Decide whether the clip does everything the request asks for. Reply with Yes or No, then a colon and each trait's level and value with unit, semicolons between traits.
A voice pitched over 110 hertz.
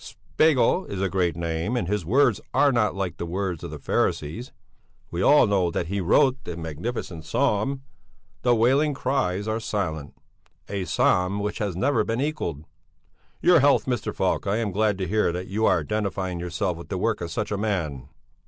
No: low, 100 Hz